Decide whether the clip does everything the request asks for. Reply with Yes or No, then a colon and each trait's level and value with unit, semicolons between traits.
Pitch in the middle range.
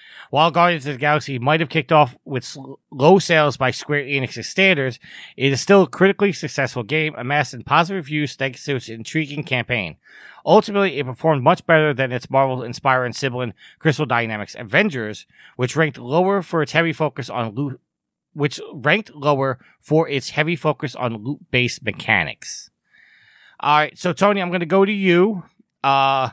Yes: medium, 150 Hz